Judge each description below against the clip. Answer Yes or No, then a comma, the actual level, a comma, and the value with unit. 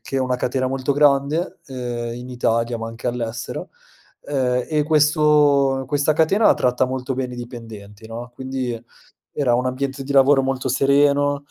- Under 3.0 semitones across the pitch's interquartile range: Yes, narrow, 2.5 semitones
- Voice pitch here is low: Yes, low, 130 Hz